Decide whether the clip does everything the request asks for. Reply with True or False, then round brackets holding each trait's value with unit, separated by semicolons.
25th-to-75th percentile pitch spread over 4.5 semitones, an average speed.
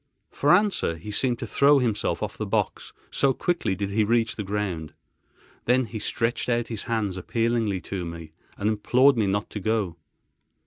False (3.2 semitones; 180 wpm)